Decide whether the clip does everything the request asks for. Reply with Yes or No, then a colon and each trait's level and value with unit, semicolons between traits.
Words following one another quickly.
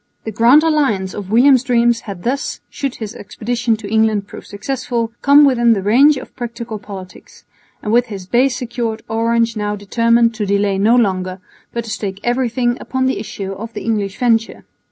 No: average, 180 wpm